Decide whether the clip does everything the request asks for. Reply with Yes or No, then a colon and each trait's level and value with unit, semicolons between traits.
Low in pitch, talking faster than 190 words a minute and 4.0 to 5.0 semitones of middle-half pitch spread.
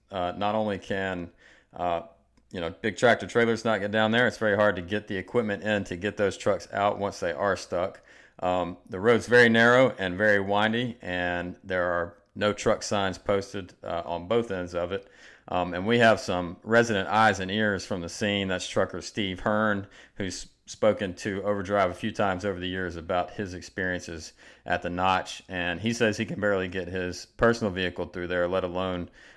No: very low, 95 Hz; average, 200 wpm; average, 2.9 semitones